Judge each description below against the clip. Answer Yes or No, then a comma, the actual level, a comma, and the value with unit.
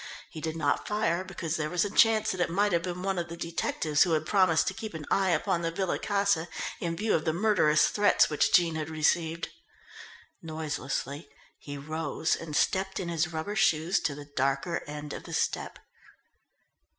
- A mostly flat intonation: No, average, 3.4 semitones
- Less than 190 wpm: No, average, 195 wpm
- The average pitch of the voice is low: No, medium, 170 Hz